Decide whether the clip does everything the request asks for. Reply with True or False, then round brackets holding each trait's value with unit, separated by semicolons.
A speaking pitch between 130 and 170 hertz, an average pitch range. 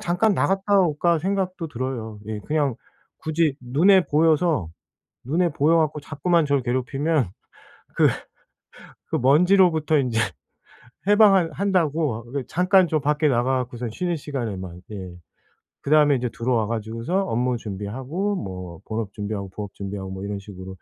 False (140 Hz; 7.2 semitones)